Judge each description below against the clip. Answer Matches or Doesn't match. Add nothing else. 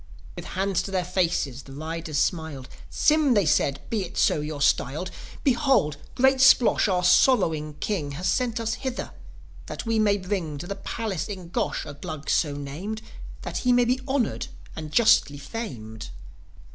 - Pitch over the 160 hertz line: Matches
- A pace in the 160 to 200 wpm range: Matches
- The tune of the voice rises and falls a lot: Matches